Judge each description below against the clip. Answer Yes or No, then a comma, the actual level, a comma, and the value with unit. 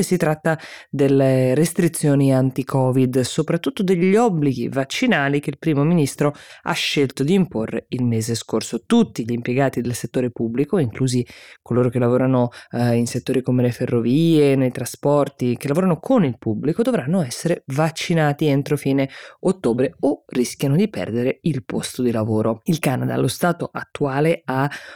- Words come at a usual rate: Yes, average, 150 wpm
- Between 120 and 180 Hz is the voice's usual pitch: Yes, low, 135 Hz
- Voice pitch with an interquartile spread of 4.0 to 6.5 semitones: Yes, average, 4.3 semitones